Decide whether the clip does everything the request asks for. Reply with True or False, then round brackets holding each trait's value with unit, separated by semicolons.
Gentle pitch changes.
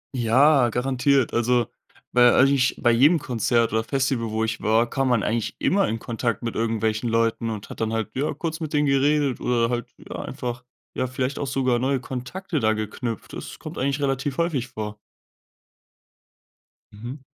False (3.1 semitones)